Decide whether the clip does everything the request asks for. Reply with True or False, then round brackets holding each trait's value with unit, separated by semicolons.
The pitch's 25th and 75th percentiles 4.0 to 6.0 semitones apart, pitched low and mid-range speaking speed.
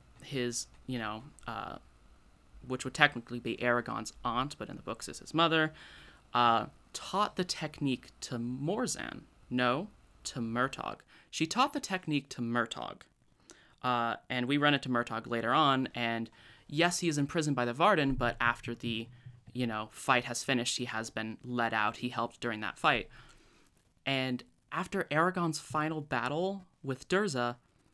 True (4.3 semitones; 125 Hz; 160 wpm)